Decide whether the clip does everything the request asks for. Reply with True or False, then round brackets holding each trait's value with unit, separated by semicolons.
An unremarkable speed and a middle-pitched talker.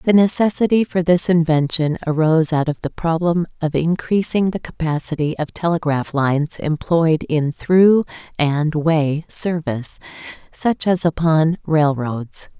False (130 wpm; 160 Hz)